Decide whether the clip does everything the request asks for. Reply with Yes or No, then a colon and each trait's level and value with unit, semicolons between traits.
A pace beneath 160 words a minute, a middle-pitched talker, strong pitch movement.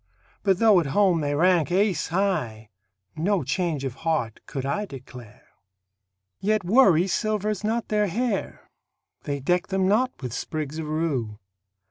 Yes: average, 145 wpm; medium, 175 Hz; wide, 6.0 semitones